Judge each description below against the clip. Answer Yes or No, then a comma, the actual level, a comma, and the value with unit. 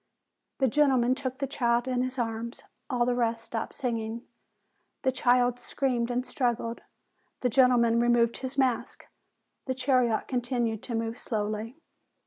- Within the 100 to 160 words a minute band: Yes, average, 145 wpm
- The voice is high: Yes, high, 245 Hz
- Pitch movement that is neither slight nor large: No, narrow, 1.8 semitones